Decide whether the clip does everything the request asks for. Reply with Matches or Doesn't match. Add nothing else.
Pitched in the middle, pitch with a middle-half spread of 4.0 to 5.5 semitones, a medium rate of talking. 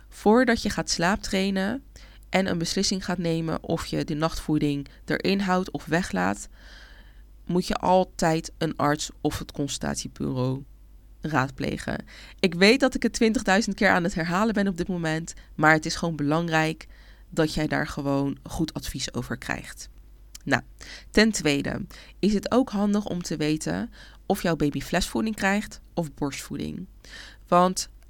Matches